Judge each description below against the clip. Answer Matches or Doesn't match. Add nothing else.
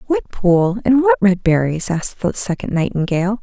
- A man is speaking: Doesn't match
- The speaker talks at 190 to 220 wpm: Doesn't match